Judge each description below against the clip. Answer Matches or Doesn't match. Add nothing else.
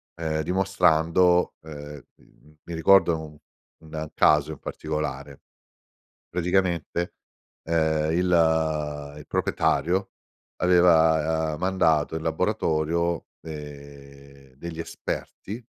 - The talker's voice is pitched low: Matches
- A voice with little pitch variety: Matches